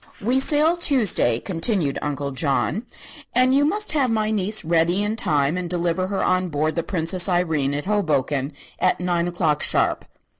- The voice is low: No, medium, 180 Hz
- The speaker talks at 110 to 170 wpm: Yes, average, 165 wpm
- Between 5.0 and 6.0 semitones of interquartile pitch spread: Yes, wide, 5.6 semitones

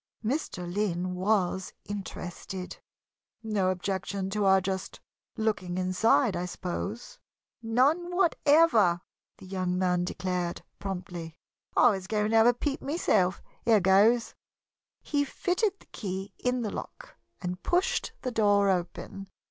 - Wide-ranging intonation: No, average, 4.3 semitones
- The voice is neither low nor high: No, high, 195 Hz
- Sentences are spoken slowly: Yes, slow, 130 wpm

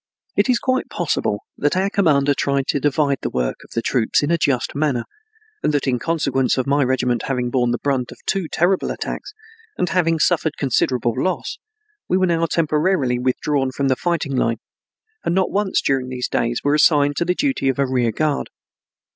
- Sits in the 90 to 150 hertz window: Yes, medium, 140 Hz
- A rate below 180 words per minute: No, average, 195 wpm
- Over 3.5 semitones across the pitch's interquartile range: Yes, average, 4.5 semitones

